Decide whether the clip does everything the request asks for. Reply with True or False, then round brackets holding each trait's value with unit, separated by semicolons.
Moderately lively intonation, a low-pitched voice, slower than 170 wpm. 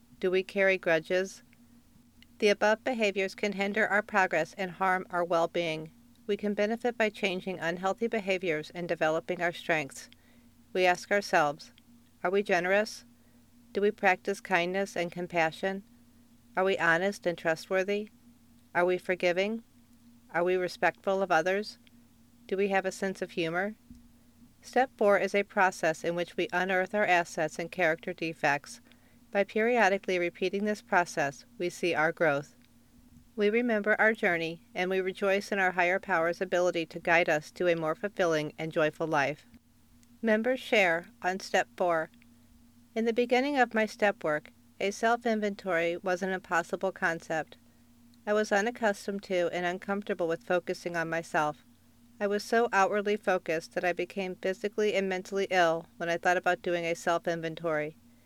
False (3.5 semitones; 185 Hz; 160 wpm)